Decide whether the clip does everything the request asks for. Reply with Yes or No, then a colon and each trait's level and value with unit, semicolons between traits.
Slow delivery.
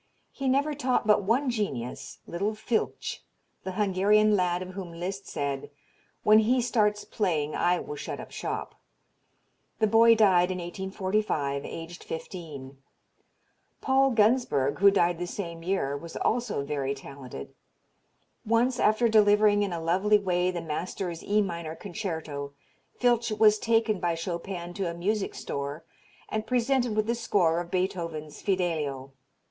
No: average, 145 wpm